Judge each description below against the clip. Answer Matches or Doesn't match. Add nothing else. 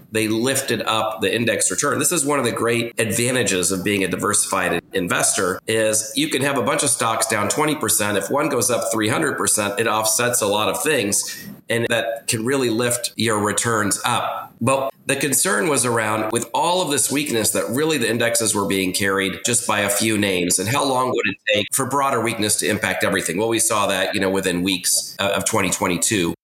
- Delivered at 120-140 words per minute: Doesn't match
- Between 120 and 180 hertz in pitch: Doesn't match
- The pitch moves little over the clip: Doesn't match